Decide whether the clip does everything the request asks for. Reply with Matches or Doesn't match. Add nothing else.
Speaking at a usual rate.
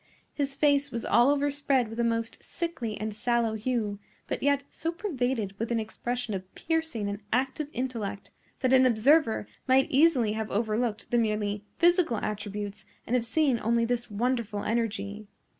Matches